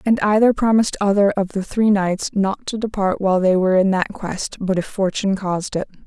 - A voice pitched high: Yes, high, 195 Hz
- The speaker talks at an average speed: No, fast, 220 wpm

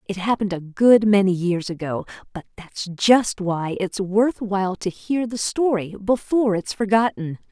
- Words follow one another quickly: No, average, 175 wpm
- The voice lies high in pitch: Yes, high, 200 Hz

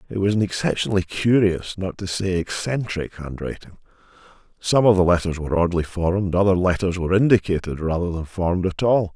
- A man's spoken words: Yes, male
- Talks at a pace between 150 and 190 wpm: Yes, average, 165 wpm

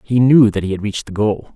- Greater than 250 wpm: Yes, fast, 310 wpm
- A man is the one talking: Yes, male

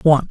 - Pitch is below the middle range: No, medium, 150 Hz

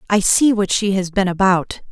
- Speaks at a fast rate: Yes, fast, 220 wpm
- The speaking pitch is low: No, high, 195 Hz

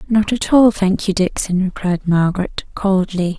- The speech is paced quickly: No, average, 160 wpm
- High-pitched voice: Yes, high, 195 Hz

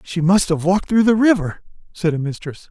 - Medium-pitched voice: Yes, medium, 180 Hz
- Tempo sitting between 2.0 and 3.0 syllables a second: No, 5.6 syllables/s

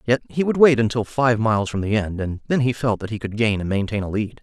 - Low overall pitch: Yes, low, 110 Hz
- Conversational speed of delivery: No, fast, 300 wpm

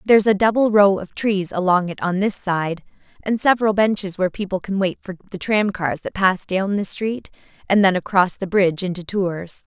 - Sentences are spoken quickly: Yes, fast, 210 wpm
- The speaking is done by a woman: Yes, female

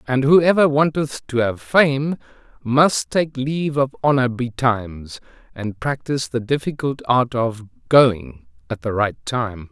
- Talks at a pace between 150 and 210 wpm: No, slow, 135 wpm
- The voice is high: No, low, 125 Hz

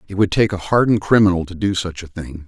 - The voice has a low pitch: Yes, very low, 95 Hz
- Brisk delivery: Yes, fast, 265 wpm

